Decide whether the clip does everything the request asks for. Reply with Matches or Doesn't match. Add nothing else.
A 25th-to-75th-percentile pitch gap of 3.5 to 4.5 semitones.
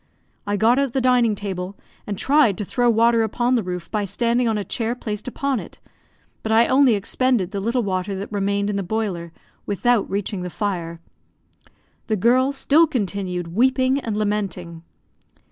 Matches